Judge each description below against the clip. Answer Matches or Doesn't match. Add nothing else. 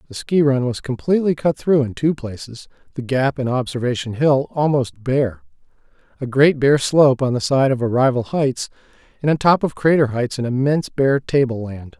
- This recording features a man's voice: Matches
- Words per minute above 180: Matches